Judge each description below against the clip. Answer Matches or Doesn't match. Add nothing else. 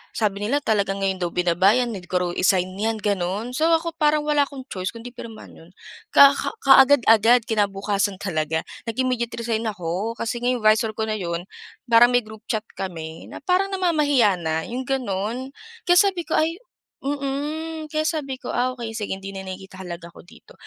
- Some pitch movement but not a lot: Doesn't match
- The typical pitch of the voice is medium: Doesn't match